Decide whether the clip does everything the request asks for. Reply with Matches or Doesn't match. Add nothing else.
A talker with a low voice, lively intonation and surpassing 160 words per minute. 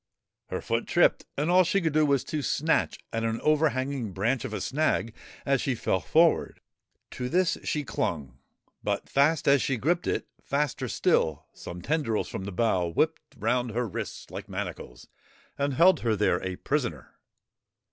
Matches